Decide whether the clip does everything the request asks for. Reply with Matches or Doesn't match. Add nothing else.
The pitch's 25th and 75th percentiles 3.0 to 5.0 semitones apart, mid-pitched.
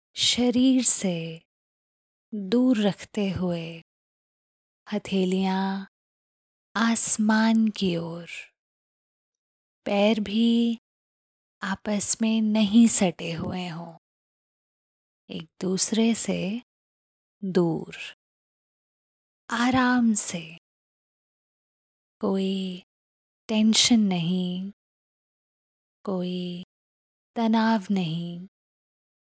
Doesn't match